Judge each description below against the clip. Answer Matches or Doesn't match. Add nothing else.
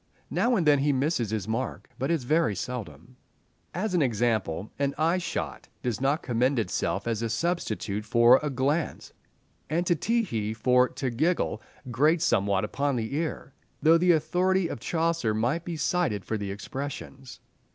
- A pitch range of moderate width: Doesn't match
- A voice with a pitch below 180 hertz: Matches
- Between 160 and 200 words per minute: Matches